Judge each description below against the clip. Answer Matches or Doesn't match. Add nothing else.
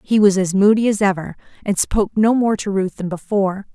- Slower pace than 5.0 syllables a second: Doesn't match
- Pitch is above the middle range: Matches